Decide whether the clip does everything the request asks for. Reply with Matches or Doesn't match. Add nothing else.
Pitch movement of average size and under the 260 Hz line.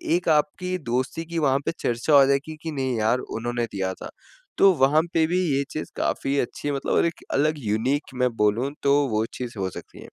Matches